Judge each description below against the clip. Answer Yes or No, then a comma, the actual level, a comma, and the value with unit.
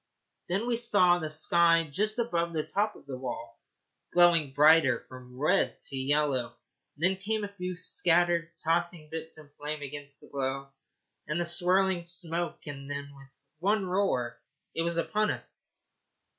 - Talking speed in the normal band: Yes, average, 155 wpm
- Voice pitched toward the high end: No, medium, 165 Hz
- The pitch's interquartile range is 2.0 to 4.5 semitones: Yes, average, 4.1 semitones